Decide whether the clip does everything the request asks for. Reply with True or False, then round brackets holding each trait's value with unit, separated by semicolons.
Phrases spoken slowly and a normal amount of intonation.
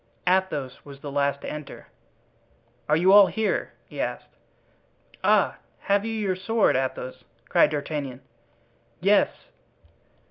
False (120 wpm; 5.9 semitones)